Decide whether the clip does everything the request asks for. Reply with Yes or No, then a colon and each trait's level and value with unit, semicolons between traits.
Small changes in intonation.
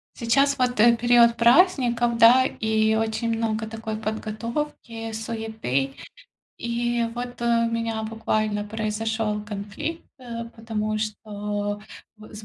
Yes: narrow, 1.6 semitones